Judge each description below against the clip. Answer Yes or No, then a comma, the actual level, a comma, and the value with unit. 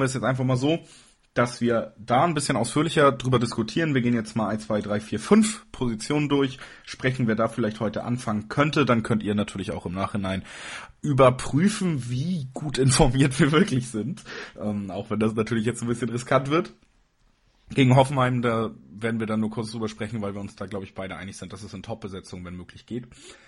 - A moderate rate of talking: No, fast, 205 wpm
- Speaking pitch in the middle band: No, low, 120 Hz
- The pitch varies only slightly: No, average, 4.0 semitones